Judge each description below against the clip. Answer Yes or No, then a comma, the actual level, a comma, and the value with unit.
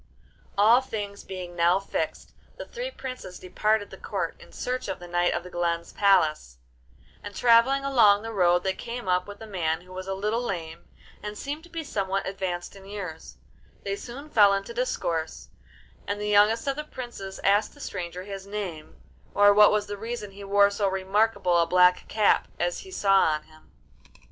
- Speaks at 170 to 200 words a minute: Yes, average, 190 wpm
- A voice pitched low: No, high, 200 Hz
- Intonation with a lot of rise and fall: No, average, 3.4 semitones